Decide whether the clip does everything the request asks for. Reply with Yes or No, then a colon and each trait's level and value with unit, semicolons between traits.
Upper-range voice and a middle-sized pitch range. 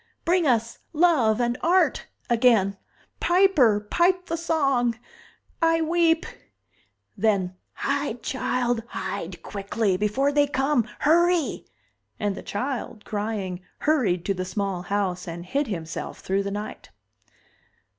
No: high, 235 Hz; wide, 7.0 semitones